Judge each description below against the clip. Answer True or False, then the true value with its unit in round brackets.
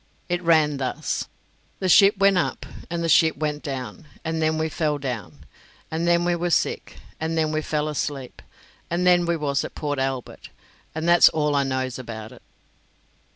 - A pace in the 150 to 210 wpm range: True (185 wpm)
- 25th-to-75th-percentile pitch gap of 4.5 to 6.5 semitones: False (3.5 semitones)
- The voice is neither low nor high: True (155 Hz)